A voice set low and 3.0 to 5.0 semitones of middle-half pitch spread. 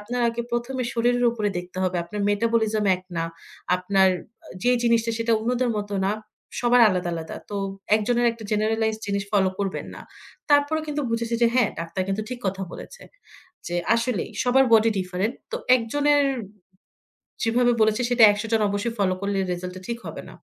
No: high, 220 Hz; average, 3.3 semitones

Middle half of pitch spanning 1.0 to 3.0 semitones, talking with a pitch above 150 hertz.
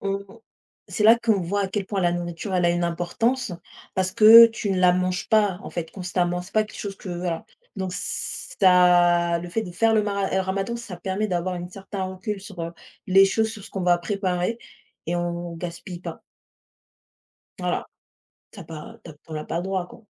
Yes: narrow, 2.6 semitones; medium, 185 Hz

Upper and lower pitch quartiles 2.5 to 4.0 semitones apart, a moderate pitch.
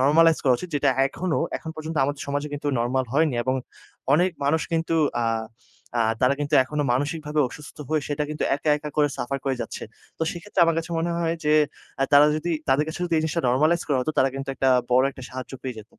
Yes: average, 3.1 semitones; medium, 150 Hz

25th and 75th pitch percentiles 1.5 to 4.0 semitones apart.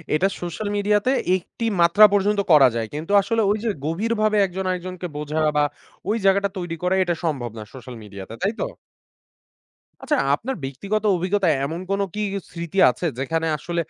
No: average, 4.9 semitones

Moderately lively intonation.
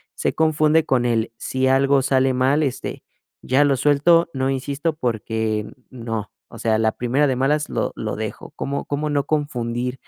Yes: average, 3.2 semitones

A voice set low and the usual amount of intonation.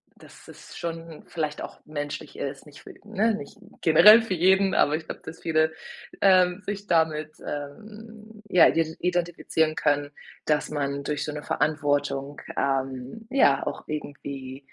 No: medium, 155 Hz; average, 4.3 semitones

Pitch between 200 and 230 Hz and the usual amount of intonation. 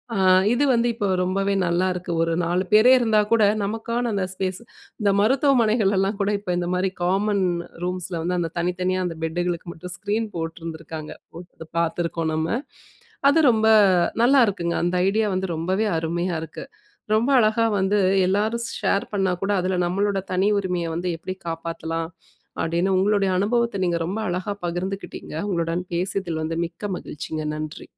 No: medium, 185 Hz; average, 3.3 semitones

